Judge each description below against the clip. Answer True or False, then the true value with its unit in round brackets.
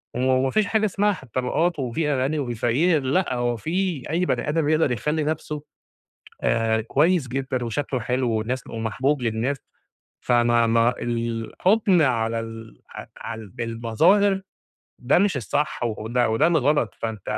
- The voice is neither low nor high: False (130 Hz)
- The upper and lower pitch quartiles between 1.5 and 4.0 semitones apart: False (5.2 semitones)